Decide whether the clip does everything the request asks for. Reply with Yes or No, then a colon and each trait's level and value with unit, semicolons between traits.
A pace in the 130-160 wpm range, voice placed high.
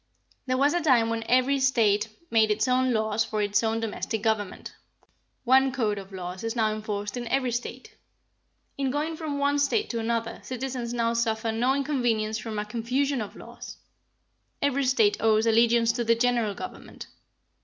No: average, 175 wpm; high, 230 Hz